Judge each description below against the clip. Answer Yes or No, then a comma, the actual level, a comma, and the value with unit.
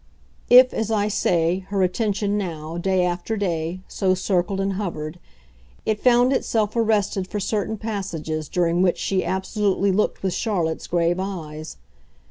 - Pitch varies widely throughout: No, average, 3.3 semitones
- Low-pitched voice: No, high, 190 Hz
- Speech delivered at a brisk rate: No, average, 145 wpm